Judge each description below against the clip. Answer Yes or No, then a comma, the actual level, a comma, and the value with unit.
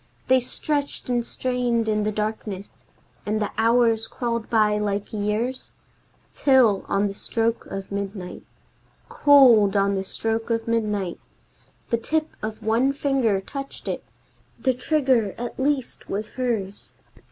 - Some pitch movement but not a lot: Yes, average, 3.4 semitones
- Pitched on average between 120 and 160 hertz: No, high, 225 Hz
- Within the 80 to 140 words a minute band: Yes, slow, 135 wpm